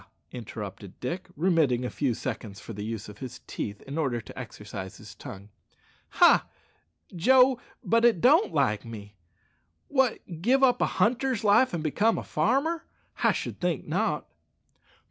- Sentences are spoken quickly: No, average, 155 wpm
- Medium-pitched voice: Yes, medium, 145 Hz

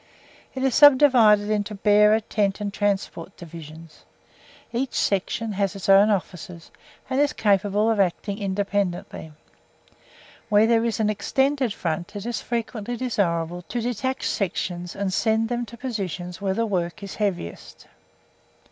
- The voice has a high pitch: Yes, high, 205 Hz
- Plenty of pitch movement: No, average, 3.3 semitones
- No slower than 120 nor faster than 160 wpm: Yes, average, 140 wpm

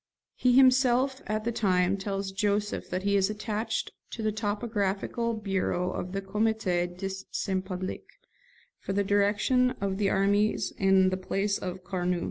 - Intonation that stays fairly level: Yes, narrow, 2.1 semitones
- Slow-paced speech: No, average, 155 wpm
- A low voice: No, high, 200 Hz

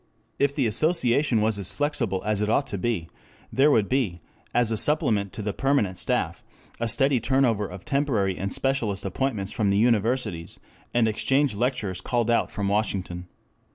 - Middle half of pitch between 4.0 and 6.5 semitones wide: Yes, average, 5.0 semitones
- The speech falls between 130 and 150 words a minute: No, average, 170 wpm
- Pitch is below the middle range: Yes, low, 110 Hz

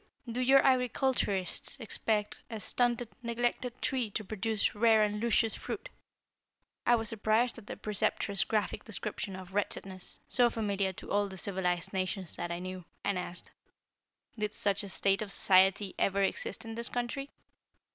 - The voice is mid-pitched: No, high, 210 Hz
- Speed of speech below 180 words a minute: Yes, average, 155 wpm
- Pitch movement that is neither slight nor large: Yes, average, 3.3 semitones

